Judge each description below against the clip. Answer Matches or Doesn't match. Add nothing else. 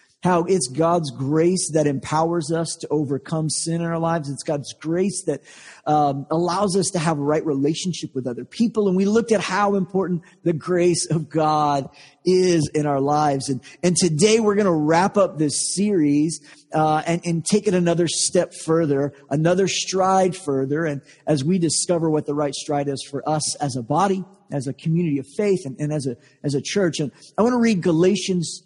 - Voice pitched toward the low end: Doesn't match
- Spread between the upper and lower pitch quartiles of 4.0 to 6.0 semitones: Doesn't match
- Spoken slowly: Doesn't match